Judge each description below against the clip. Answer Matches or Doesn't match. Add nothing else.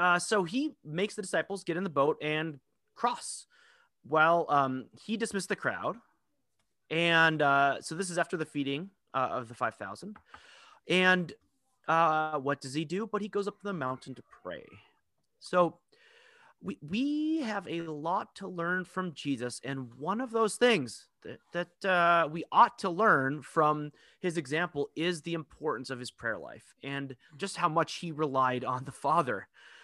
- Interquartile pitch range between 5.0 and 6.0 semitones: Matches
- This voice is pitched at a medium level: Matches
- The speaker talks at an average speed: Matches